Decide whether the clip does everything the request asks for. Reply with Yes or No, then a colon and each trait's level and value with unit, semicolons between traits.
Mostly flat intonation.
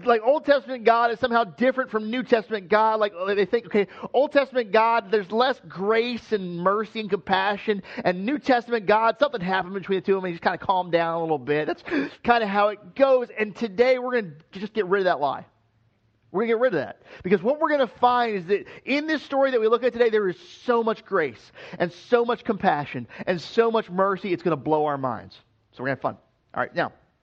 No: average, 4.6 semitones